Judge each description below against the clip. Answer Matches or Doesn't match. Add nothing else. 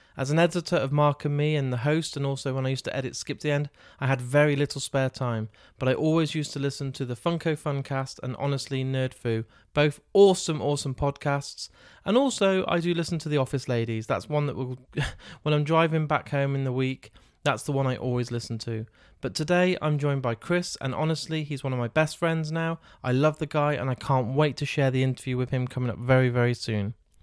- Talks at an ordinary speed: Doesn't match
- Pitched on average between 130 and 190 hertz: Matches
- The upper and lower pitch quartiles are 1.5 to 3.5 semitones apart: Matches